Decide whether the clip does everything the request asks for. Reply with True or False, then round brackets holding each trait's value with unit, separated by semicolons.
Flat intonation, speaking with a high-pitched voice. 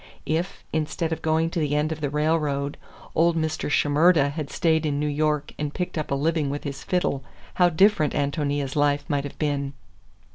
False (2.0 semitones; 150 Hz)